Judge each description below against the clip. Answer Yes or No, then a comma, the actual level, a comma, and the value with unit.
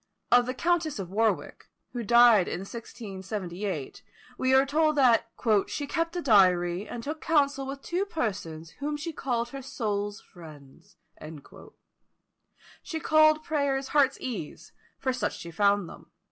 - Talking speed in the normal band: Yes, average, 145 wpm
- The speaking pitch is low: No, high, 240 Hz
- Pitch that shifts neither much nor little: No, wide, 6.4 semitones